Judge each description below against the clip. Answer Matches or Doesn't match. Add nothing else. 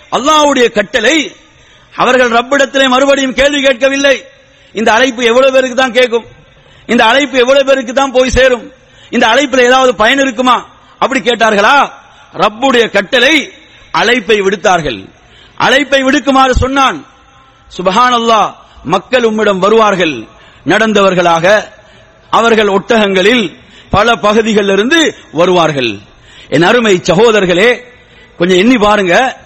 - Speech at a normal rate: Doesn't match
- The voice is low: Doesn't match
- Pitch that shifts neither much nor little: Matches